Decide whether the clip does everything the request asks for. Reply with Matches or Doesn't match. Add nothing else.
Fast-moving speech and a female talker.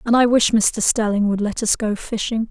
Matches